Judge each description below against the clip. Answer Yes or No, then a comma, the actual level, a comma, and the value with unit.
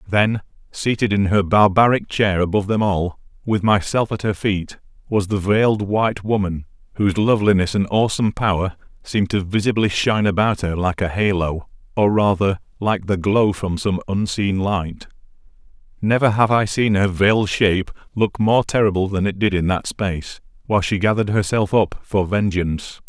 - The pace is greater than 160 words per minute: Yes, average, 170 wpm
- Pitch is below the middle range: Yes, low, 100 Hz